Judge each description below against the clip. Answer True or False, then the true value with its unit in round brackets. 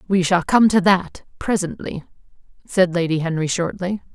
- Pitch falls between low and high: True (180 Hz)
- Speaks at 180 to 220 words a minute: False (145 wpm)